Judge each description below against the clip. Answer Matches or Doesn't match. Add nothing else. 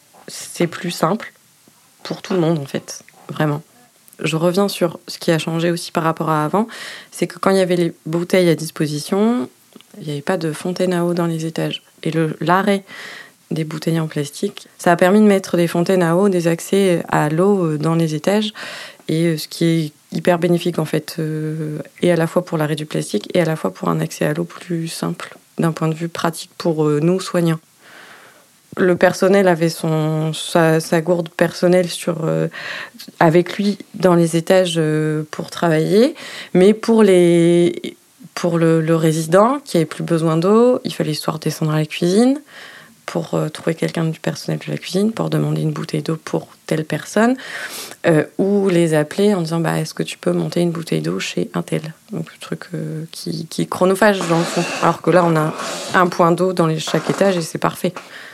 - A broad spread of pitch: Doesn't match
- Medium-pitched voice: Matches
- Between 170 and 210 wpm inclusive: Matches